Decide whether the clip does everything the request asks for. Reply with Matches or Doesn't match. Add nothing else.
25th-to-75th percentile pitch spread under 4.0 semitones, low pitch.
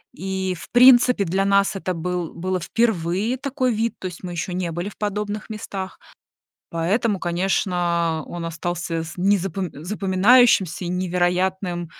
Doesn't match